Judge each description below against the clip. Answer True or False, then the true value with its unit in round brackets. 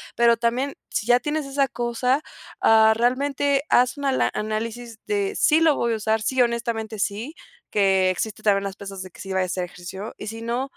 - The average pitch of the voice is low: False (235 Hz)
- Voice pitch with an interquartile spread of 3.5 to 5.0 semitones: True (3.8 semitones)